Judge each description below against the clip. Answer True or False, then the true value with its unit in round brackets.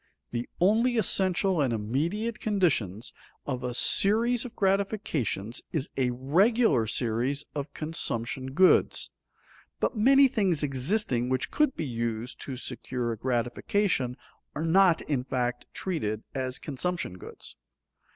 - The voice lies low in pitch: False (145 Hz)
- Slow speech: True (125 wpm)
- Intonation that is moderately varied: False (8.1 semitones)